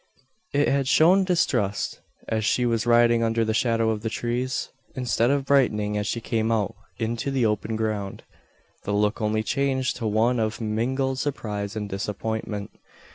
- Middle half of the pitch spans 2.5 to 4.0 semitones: Yes, average, 3.1 semitones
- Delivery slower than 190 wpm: Yes, average, 165 wpm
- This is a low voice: Yes, low, 115 Hz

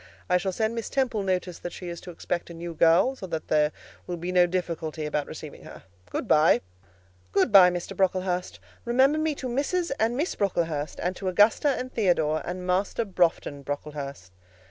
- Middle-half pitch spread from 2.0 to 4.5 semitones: No, average, 4.9 semitones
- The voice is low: No, medium, 180 Hz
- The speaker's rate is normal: Yes, average, 190 wpm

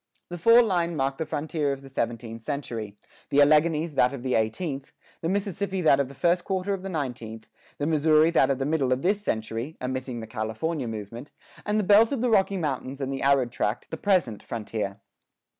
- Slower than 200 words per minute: No, fast, 205 wpm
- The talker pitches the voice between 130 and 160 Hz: Yes, medium, 140 Hz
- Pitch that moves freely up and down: Yes, wide, 6.0 semitones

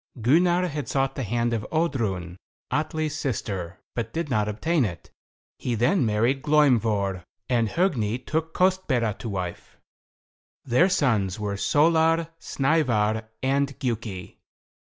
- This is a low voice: Yes, low, 125 Hz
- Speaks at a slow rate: Yes, slow, 125 wpm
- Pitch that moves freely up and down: Yes, wide, 6.5 semitones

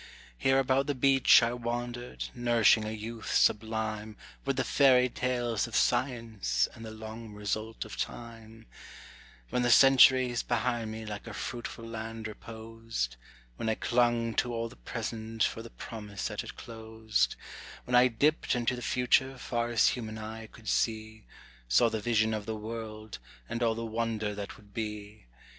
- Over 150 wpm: Yes, average, 165 wpm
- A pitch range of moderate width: No, narrow, 1.7 semitones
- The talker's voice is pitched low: Yes, low, 115 Hz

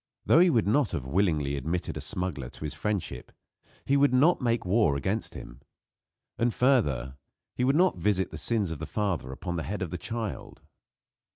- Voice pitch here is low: Yes, very low, 95 Hz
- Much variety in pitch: Yes, wide, 7.2 semitones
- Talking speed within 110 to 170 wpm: No, average, 190 wpm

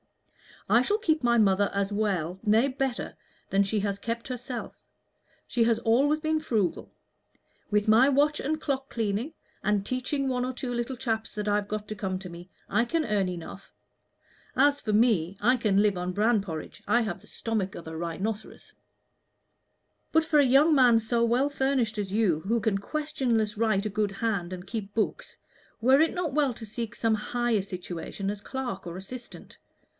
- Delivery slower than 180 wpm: No, average, 185 wpm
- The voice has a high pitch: Yes, high, 225 Hz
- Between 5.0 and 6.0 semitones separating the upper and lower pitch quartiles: No, average, 4.3 semitones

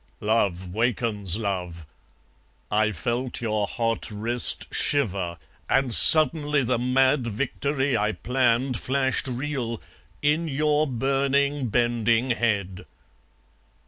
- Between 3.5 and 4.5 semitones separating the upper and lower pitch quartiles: Yes, average, 4.0 semitones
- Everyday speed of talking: No, slow, 100 wpm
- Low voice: Yes, low, 120 Hz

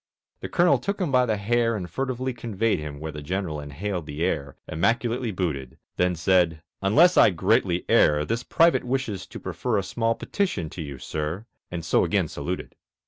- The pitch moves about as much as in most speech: No, wide, 7.1 semitones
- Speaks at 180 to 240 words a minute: Yes, average, 185 wpm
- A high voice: No, very low, 95 Hz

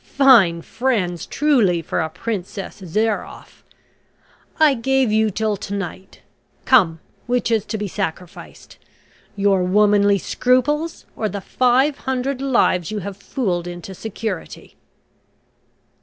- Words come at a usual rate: No, slow, 120 wpm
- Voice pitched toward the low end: No, high, 210 Hz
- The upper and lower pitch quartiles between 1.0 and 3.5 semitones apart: No, wide, 5.4 semitones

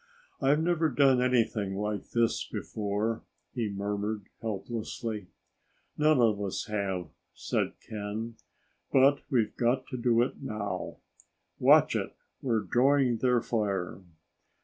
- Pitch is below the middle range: Yes, low, 115 Hz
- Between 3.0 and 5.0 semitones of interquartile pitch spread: Yes, average, 3.7 semitones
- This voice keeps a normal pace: No, slow, 120 wpm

